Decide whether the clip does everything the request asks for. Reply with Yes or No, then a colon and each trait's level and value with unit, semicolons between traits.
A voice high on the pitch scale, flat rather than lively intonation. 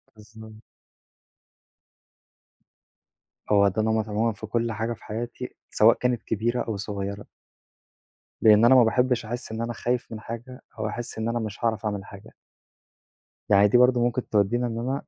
No: low, 110 Hz; narrow, 2.0 semitones